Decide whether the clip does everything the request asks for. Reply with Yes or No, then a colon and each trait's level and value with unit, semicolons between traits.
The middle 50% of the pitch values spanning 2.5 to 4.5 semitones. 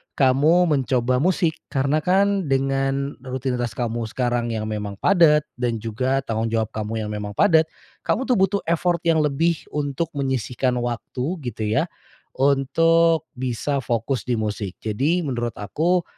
No: average, 5.3 semitones